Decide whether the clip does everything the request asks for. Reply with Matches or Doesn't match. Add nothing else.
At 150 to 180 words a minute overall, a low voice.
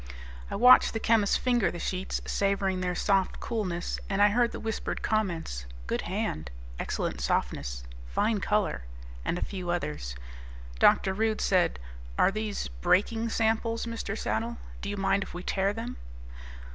Doesn't match